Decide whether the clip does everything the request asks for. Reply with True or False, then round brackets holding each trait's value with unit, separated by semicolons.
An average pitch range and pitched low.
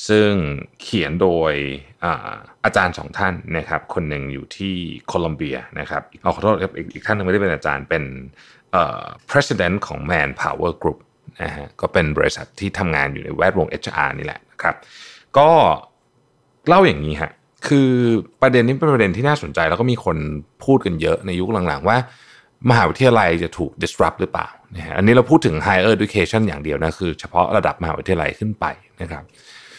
False (6.7 semitones; 95 Hz)